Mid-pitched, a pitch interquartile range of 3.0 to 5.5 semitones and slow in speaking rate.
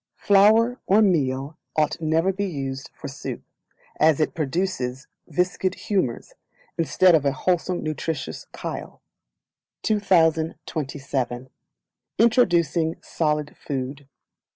Yes: medium, 160 Hz; average, 4.9 semitones; slow, 105 wpm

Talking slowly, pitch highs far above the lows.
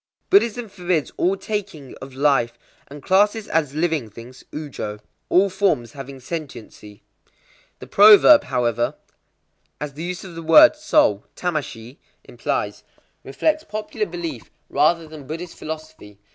Yes: slow, 120 wpm; wide, 6.3 semitones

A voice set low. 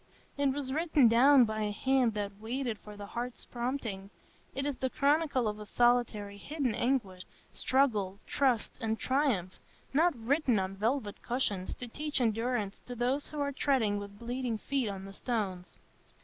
No: high, 240 Hz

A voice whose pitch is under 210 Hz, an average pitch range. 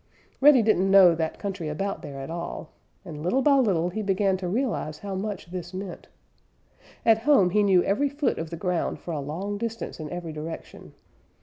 Yes: high, 190 Hz; average, 4.1 semitones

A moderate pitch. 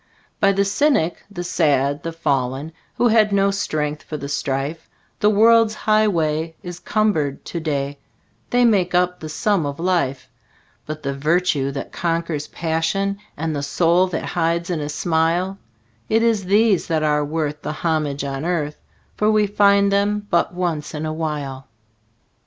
Yes: medium, 165 Hz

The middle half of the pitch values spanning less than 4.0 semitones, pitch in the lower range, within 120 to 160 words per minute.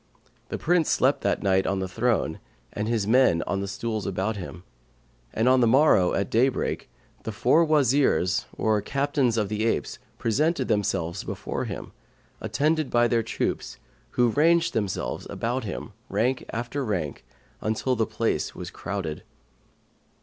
No: average, 4.7 semitones; low, 115 Hz; average, 150 wpm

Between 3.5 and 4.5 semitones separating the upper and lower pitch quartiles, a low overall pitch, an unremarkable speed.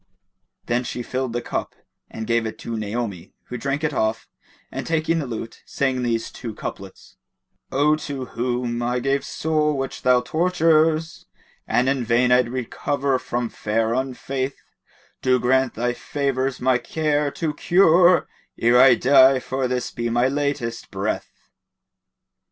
No: average, 2.9 semitones; low, 130 Hz; average, 155 wpm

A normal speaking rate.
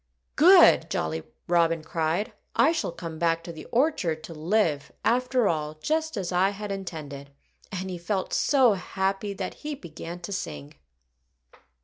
Yes: average, 150 wpm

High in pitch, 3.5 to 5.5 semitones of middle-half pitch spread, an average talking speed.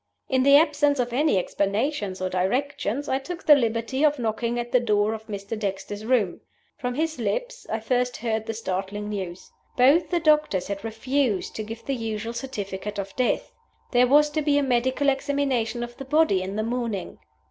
Yes: high, 240 Hz; average, 5.1 semitones; average, 190 wpm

